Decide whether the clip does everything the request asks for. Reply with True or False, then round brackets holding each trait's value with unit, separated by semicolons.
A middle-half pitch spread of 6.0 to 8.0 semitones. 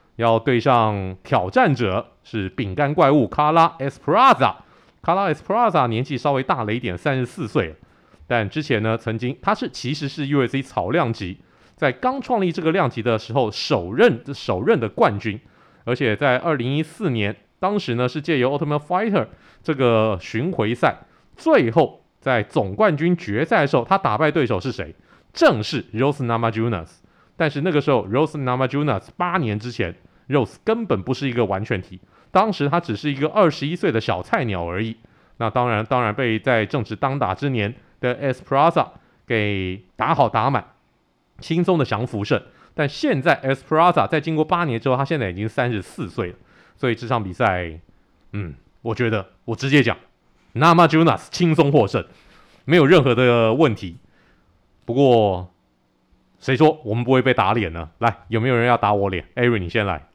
False (5.6 semitones)